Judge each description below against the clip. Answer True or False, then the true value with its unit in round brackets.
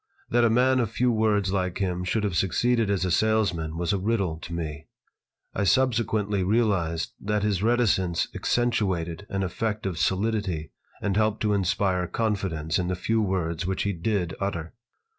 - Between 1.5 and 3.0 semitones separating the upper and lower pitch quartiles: False (3.7 semitones)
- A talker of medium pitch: False (100 Hz)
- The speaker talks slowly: False (170 wpm)